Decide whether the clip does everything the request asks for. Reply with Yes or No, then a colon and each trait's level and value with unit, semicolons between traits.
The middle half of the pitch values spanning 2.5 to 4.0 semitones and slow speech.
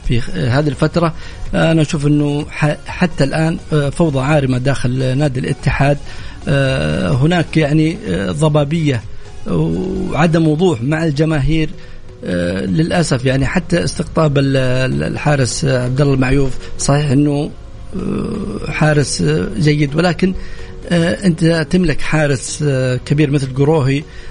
Yes: average, 3.1 semitones; slow, 95 wpm